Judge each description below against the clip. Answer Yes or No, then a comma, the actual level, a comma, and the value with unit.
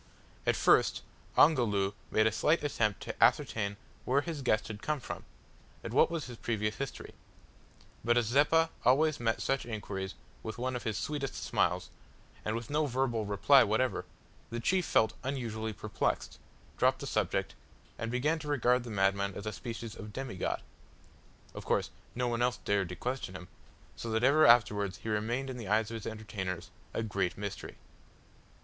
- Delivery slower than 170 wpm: No, average, 175 wpm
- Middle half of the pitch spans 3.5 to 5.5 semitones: Yes, average, 4.0 semitones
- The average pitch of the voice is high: No, low, 115 Hz